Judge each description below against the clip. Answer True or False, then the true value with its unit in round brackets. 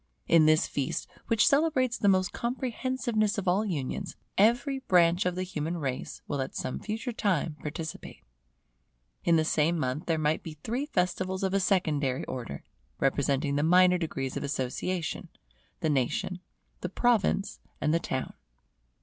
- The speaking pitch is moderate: True (175 Hz)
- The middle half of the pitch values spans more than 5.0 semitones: True (5.4 semitones)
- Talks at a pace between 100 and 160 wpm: True (155 wpm)